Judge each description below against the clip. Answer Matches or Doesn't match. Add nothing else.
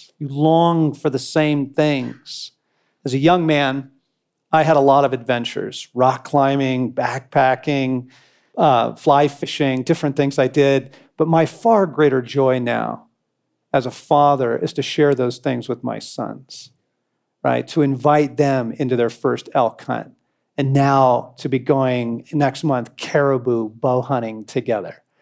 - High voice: Doesn't match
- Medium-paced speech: Matches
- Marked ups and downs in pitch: Doesn't match